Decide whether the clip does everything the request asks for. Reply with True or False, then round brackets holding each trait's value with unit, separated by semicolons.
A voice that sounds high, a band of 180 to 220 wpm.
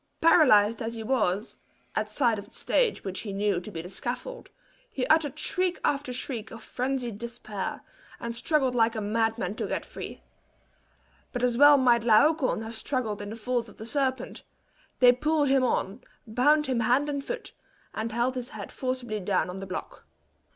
True (240 Hz; 185 wpm)